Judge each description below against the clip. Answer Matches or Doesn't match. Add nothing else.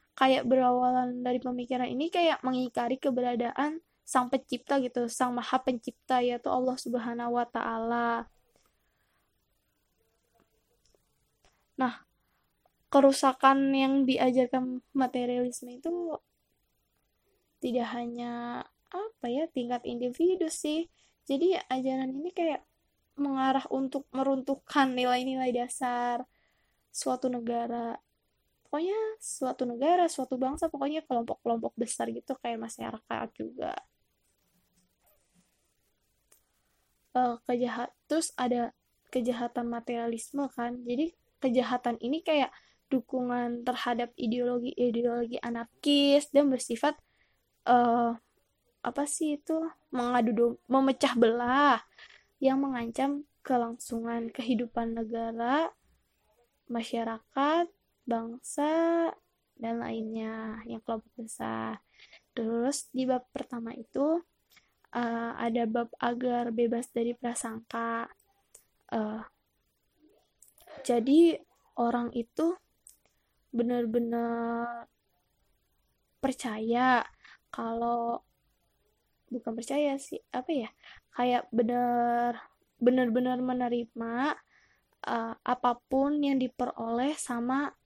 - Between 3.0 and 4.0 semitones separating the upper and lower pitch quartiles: Doesn't match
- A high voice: Matches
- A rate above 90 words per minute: Doesn't match